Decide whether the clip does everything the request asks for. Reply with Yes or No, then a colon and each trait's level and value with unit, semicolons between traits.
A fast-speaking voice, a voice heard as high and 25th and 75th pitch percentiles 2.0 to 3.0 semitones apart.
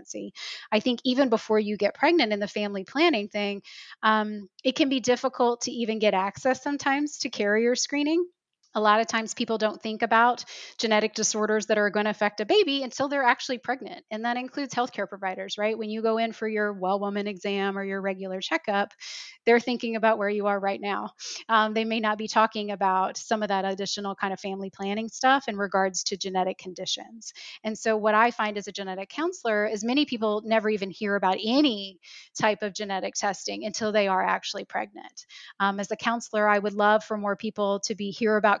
Yes: fast, 210 wpm; high, 215 Hz; average, 2.7 semitones